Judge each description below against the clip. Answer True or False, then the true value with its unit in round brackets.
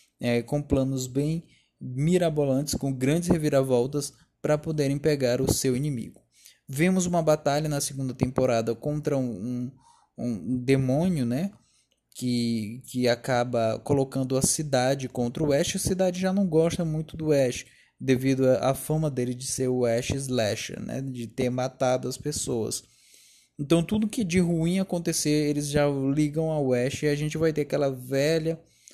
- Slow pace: False (155 wpm)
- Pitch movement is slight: False (3.4 semitones)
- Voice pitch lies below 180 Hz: True (140 Hz)